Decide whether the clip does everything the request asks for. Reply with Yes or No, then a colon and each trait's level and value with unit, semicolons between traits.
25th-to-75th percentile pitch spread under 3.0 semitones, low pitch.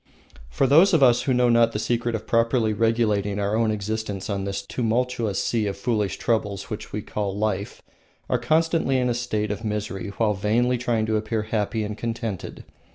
Yes: narrow, 2.4 semitones; low, 110 Hz